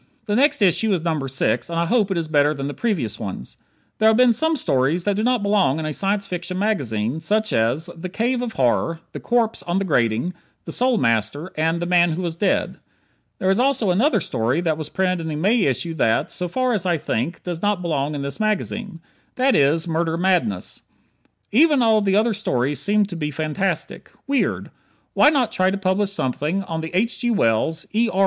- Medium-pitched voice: Yes, medium, 180 Hz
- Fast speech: Yes, fast, 215 wpm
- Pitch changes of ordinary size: No, wide, 5.8 semitones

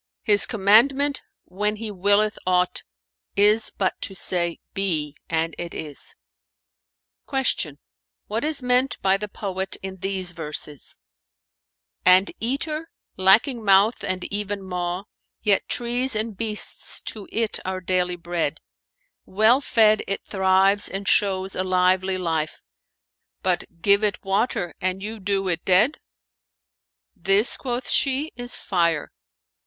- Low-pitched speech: No, high, 195 Hz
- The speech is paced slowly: Yes, slow, 130 wpm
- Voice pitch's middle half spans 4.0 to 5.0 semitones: No, average, 3.3 semitones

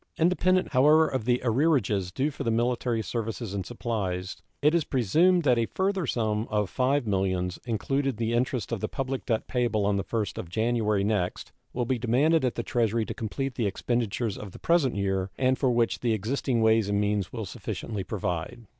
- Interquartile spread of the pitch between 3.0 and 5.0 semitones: Yes, average, 4.1 semitones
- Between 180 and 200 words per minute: Yes, average, 190 wpm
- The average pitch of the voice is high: No, low, 115 Hz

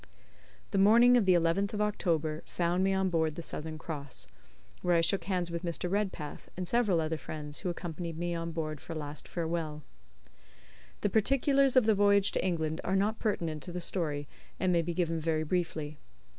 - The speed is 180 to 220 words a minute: Yes, average, 195 wpm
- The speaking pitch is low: No, medium, 170 Hz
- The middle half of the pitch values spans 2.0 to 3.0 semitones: No, average, 3.5 semitones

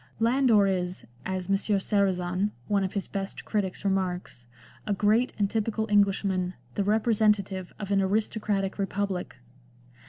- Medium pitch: No, high, 200 Hz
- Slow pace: Yes, slow, 130 wpm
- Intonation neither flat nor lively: No, narrow, 1.8 semitones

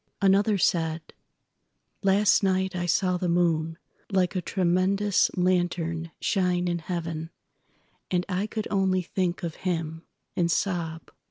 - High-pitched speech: No, medium, 180 Hz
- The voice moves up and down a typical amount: No, narrow, 2.2 semitones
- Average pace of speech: No, slow, 110 wpm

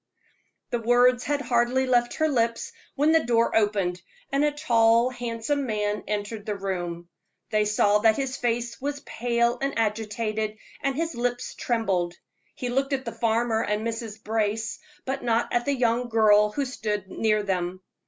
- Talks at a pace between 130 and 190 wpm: Yes, average, 165 wpm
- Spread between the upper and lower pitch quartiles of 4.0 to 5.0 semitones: No, average, 2.9 semitones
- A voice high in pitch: Yes, high, 230 Hz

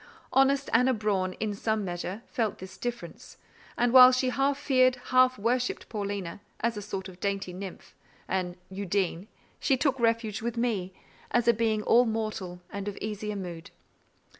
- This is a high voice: Yes, high, 215 Hz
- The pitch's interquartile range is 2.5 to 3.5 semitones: No, average, 4.0 semitones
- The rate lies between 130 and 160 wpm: Yes, average, 155 wpm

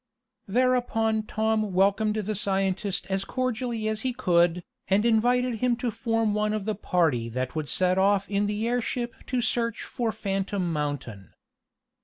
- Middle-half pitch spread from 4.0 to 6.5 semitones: No, average, 3.4 semitones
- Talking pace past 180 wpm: No, average, 155 wpm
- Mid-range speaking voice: No, high, 210 Hz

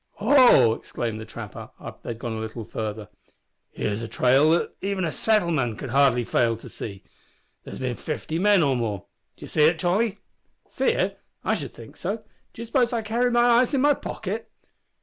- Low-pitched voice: No, medium, 155 Hz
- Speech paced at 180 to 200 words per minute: Yes, average, 195 wpm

